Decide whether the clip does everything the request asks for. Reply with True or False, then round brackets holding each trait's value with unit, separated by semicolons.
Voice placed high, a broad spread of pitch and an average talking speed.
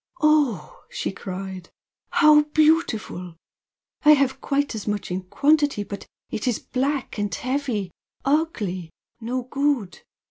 False (250 Hz; 6.8 semitones; 120 wpm)